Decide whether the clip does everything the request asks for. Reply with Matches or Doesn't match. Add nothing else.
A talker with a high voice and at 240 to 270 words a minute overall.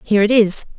Doesn't match